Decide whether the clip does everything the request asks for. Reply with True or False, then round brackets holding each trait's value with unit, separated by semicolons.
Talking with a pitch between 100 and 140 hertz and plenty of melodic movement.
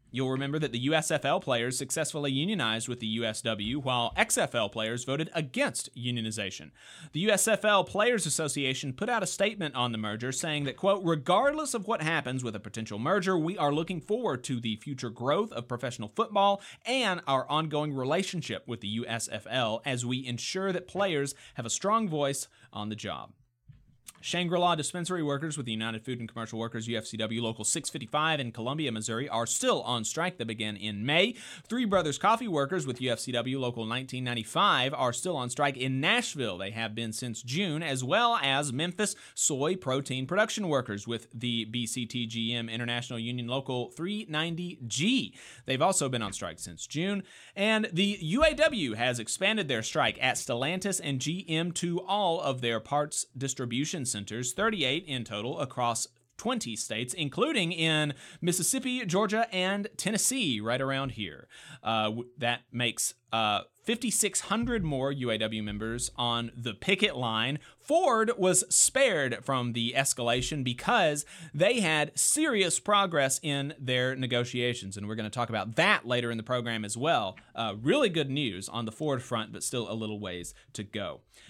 True (135 Hz; 6.9 semitones)